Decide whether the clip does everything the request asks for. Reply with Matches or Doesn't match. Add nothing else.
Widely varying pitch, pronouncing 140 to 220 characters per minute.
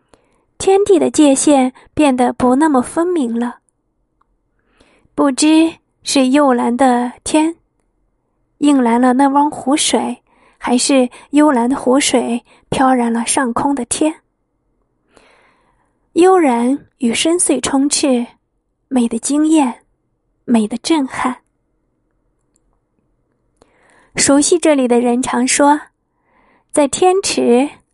Doesn't match